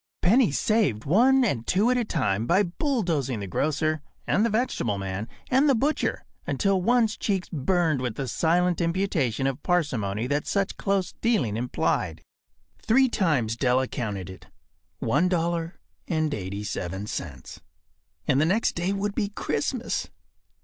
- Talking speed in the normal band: Yes, average, 150 wpm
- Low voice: No, medium, 165 Hz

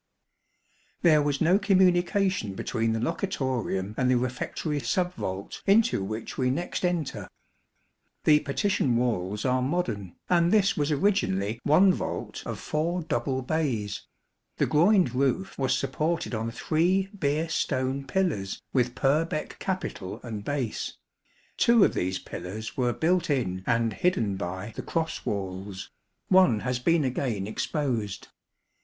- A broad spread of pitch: Yes, wide, 7.6 semitones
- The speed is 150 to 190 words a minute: No, slow, 135 wpm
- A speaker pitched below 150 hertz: Yes, low, 135 Hz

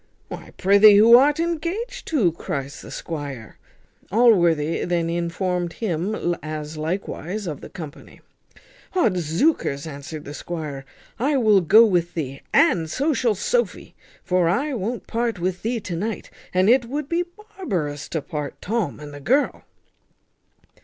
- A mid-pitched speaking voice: Yes, medium, 180 Hz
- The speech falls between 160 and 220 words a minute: No, average, 145 wpm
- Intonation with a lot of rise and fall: Yes, wide, 6.8 semitones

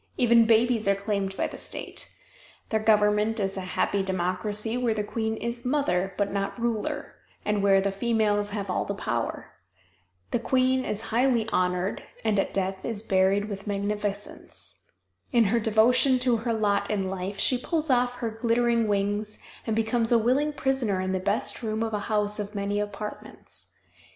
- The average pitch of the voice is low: No, high, 215 Hz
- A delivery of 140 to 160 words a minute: No, average, 175 wpm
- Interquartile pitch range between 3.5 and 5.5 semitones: No, average, 2.8 semitones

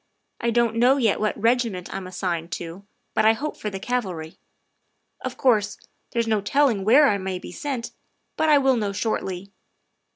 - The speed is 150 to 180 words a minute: Yes, average, 175 wpm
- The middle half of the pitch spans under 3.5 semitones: No, average, 4.3 semitones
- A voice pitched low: No, high, 220 Hz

